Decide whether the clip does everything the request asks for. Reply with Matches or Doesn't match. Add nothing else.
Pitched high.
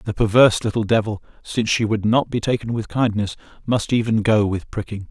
Doesn't match